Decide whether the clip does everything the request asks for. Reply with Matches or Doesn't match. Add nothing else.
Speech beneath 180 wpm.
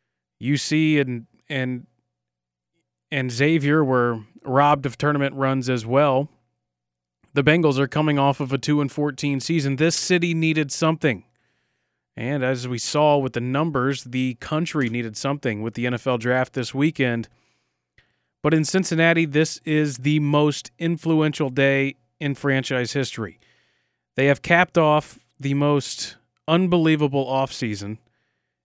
Matches